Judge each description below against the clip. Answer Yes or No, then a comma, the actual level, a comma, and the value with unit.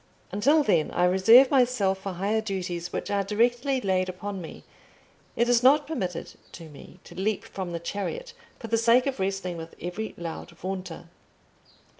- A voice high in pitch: Yes, high, 195 Hz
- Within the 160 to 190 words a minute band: Yes, average, 170 wpm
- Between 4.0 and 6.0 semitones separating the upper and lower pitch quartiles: Yes, average, 4.8 semitones